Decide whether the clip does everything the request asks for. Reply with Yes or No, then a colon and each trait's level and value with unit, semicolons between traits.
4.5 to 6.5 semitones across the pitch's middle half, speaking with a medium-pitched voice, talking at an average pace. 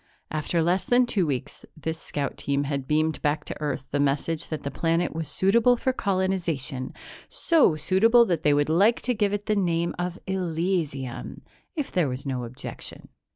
Yes: average, 4.8 semitones; medium, 165 Hz; average, 180 wpm